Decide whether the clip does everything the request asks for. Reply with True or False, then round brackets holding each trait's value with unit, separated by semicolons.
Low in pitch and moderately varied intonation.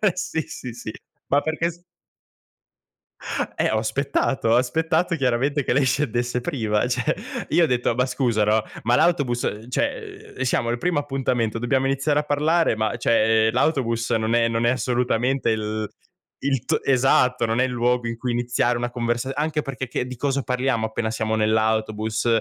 True (125 Hz; 3.1 semitones)